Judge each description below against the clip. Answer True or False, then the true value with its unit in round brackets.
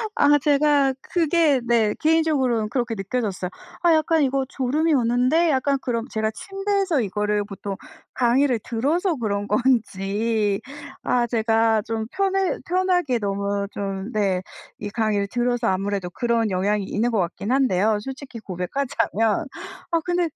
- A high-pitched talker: True (235 Hz)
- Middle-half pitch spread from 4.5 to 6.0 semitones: True (5.5 semitones)